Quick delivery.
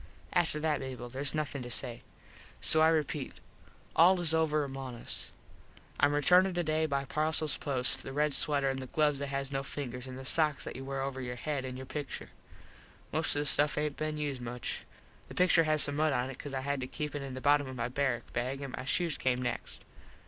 Yes: fast, 225 wpm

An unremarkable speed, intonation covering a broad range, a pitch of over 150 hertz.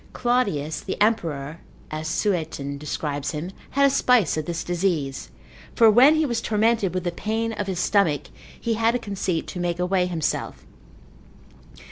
Yes: average, 160 wpm; wide, 6.0 semitones; medium, 185 Hz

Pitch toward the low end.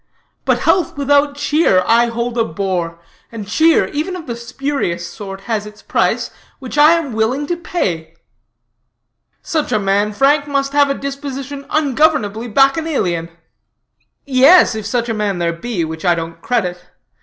No: high, 240 Hz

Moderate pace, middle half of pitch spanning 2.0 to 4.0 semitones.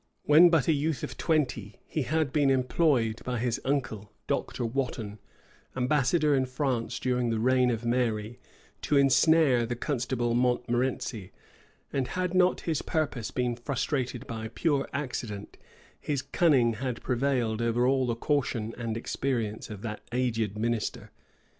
Yes: average, 145 wpm; average, 3.3 semitones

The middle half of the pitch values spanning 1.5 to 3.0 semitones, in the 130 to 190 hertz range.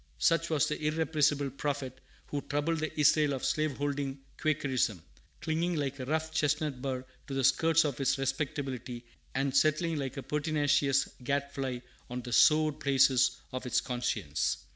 Yes: narrow, 2.5 semitones; medium, 140 Hz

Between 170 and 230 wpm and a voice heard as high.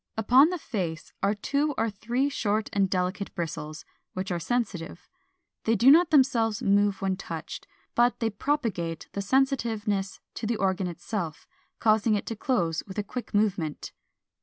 No: average, 160 wpm; high, 205 Hz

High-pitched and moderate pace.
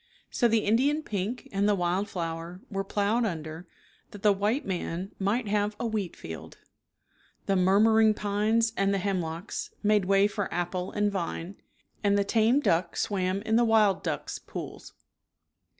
Yes: high, 200 Hz; average, 170 wpm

